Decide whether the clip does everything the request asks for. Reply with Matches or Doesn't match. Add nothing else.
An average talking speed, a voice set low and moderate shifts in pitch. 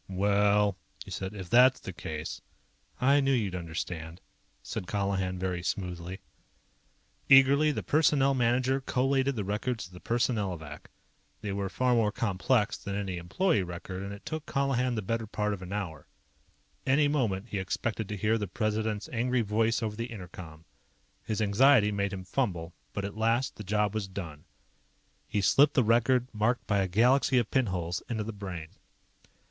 Matches